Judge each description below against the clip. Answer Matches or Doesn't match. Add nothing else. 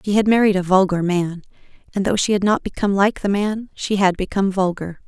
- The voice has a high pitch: Matches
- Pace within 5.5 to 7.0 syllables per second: Matches